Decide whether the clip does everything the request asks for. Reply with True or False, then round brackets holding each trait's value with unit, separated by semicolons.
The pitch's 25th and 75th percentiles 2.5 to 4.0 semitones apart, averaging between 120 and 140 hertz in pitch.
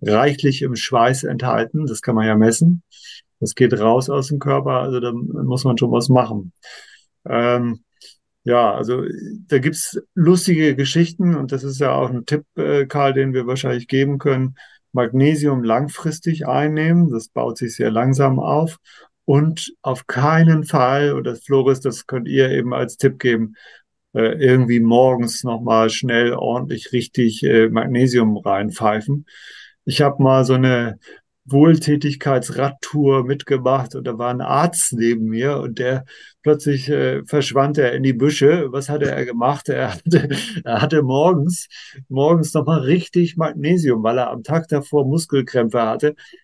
True (3.6 semitones; 135 Hz)